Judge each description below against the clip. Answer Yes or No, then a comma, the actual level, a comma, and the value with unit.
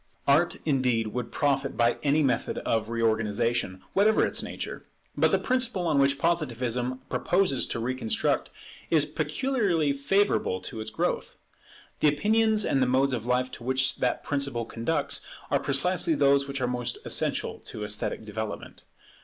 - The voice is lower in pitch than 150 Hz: Yes, low, 135 Hz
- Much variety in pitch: No, average, 4.7 semitones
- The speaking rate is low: No, average, 155 wpm